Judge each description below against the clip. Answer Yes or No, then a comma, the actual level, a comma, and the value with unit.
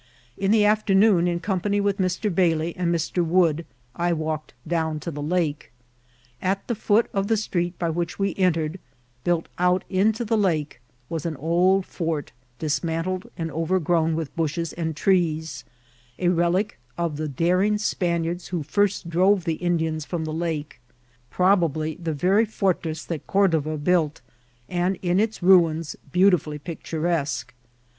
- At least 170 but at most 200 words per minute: No, average, 150 wpm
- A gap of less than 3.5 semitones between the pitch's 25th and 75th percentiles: Yes, average, 2.8 semitones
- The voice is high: No, medium, 170 Hz